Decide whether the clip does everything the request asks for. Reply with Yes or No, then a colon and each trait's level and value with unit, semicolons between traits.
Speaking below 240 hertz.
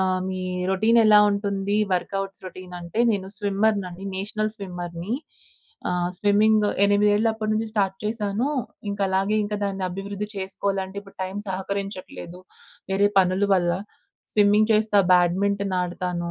Yes: high, 200 Hz